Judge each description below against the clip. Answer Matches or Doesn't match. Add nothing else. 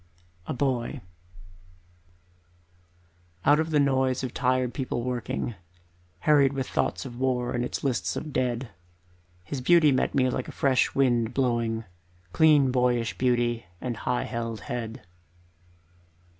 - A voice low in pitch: Matches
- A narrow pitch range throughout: Matches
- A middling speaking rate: Doesn't match